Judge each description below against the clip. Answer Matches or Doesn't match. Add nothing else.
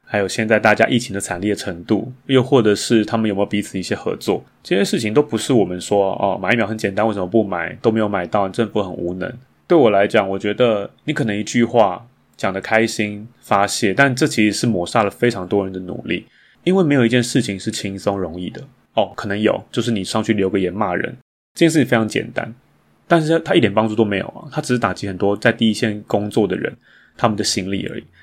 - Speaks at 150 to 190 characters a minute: Doesn't match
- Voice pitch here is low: Matches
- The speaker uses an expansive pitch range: Doesn't match